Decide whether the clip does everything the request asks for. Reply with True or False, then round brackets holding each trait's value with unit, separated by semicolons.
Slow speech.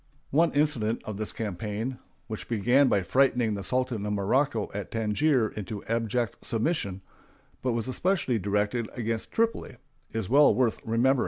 False (150 wpm)